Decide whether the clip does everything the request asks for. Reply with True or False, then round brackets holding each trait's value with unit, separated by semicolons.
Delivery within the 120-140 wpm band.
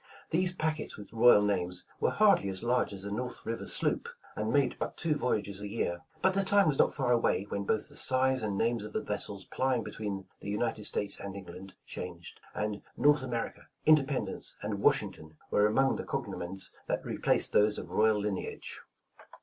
False (195 wpm)